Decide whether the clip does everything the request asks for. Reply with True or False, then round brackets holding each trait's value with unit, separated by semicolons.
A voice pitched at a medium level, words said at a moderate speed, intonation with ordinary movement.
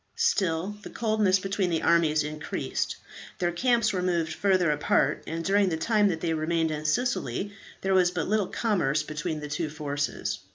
True (175 Hz; 175 wpm; 4.2 semitones)